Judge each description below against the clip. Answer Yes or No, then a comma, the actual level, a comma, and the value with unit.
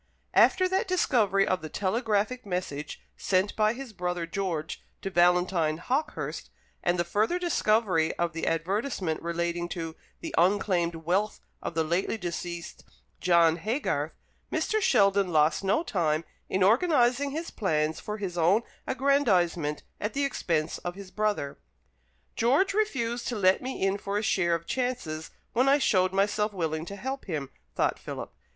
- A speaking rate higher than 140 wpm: Yes, average, 155 wpm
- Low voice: No, high, 190 Hz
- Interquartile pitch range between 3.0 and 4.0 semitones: No, wide, 5.4 semitones